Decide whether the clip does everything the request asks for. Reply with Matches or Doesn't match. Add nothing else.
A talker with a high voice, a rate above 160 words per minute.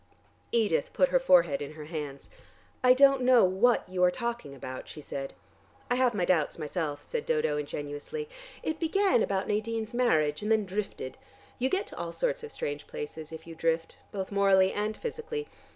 Matches